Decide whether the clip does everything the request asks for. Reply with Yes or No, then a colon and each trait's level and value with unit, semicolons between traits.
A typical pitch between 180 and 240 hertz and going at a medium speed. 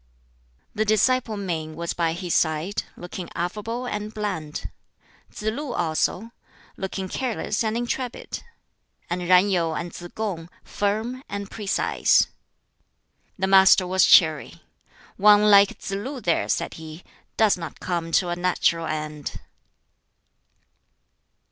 No: high, 190 Hz; slow, 125 wpm